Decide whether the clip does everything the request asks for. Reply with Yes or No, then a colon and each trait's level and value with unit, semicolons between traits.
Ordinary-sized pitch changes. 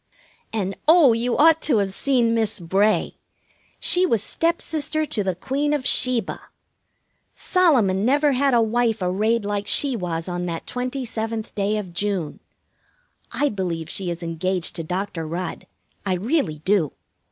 No: wide, 5.7 semitones